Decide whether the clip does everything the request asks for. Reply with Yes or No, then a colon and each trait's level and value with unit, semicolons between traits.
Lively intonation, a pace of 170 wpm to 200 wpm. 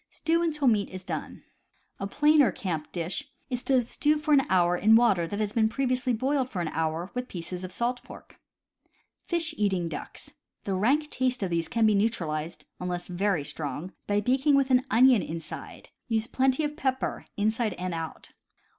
Yes: wide, 6.7 semitones; average, 185 wpm